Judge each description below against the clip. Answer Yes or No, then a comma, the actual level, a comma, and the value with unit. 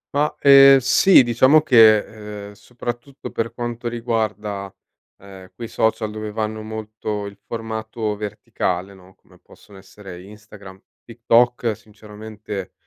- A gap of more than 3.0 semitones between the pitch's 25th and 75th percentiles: No, narrow, 2.4 semitones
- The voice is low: Yes, low, 110 Hz